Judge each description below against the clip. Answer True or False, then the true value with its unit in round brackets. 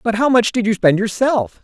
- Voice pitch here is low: False (220 Hz)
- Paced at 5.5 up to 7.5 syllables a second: False (5.2 syllables/s)